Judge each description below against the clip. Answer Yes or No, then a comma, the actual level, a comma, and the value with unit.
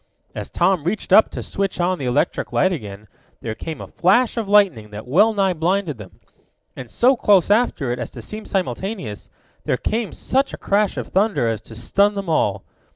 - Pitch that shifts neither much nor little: No, wide, 8.9 semitones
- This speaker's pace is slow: No, average, 200 wpm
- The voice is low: No, medium, 185 Hz